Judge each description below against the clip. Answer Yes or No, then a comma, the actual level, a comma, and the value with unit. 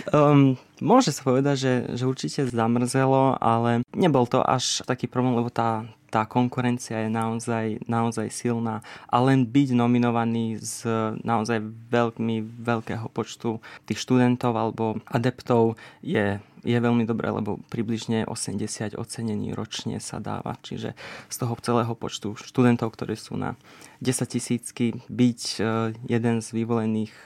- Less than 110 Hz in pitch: No, low, 115 Hz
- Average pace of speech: Yes, average, 135 wpm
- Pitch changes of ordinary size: No, narrow, 1.8 semitones